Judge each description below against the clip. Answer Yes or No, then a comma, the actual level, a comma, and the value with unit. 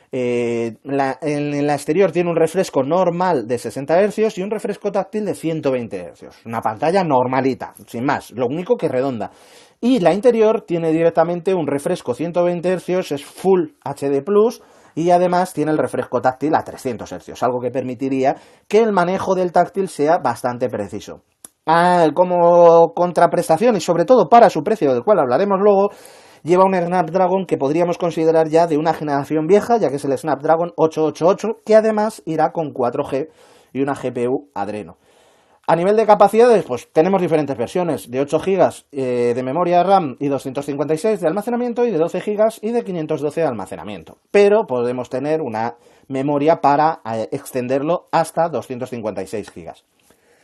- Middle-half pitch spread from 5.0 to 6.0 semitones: Yes, wide, 5.5 semitones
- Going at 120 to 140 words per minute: No, average, 165 wpm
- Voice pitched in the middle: Yes, medium, 160 Hz